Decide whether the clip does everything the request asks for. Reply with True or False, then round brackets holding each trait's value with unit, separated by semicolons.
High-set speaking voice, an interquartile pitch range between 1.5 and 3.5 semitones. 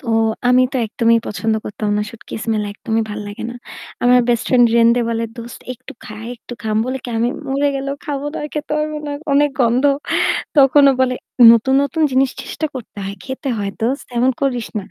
True (245 Hz; 3.2 semitones)